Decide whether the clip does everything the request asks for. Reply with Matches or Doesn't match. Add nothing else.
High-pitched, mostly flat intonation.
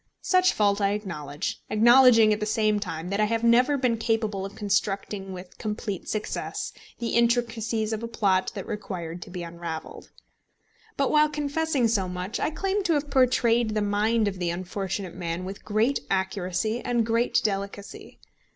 Doesn't match